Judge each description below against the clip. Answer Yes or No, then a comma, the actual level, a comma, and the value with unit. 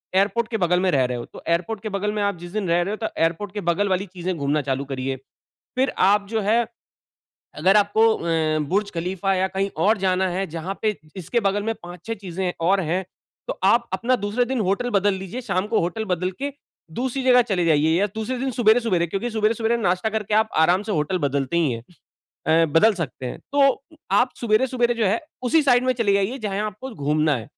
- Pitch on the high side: Yes, high, 195 Hz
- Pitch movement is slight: No, average, 4.4 semitones